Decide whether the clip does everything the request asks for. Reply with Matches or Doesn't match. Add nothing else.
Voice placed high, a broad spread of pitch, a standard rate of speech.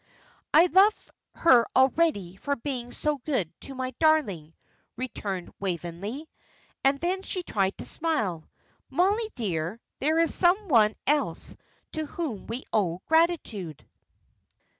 Doesn't match